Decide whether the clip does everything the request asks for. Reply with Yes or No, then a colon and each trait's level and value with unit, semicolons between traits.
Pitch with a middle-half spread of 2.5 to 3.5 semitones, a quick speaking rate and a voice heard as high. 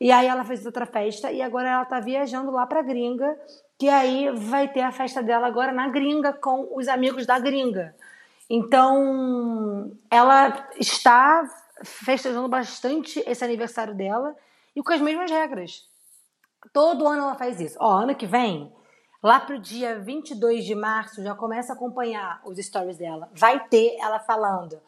No: average, 3.2 semitones; average, 165 wpm; very high, 255 Hz